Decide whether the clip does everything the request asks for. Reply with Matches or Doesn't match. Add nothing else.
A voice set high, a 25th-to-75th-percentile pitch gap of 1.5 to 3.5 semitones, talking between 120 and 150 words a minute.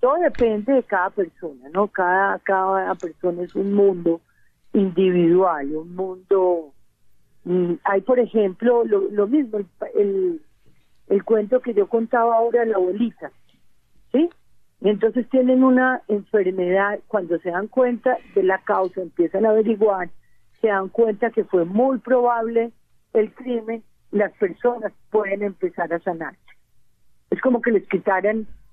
Doesn't match